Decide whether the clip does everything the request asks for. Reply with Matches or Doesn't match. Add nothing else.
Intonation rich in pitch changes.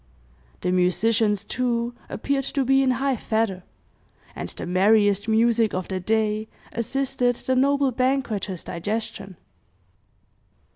Doesn't match